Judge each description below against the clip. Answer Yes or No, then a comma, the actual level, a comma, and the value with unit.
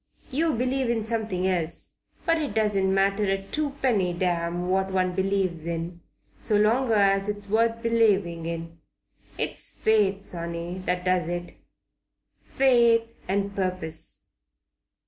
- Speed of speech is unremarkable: No, slow, 125 wpm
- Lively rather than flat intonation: No, average, 4.2 semitones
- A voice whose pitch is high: Yes, high, 195 Hz